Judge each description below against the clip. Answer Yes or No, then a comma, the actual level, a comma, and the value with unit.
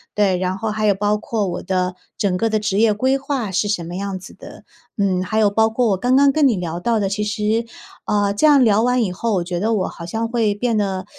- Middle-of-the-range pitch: No, high, 210 Hz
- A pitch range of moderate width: Yes, average, 3.2 semitones